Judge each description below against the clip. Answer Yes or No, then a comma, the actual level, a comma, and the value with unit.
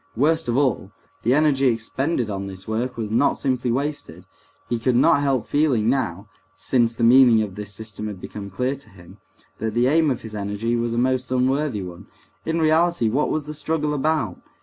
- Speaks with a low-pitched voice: Yes, low, 125 Hz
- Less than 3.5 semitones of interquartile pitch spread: No, average, 4.8 semitones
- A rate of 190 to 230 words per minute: Yes, average, 195 wpm